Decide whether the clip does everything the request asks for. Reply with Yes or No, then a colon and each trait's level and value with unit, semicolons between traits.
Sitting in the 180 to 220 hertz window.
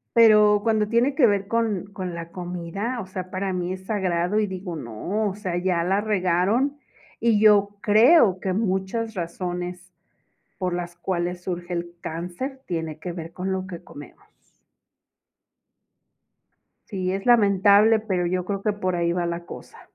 Yes: high, 190 Hz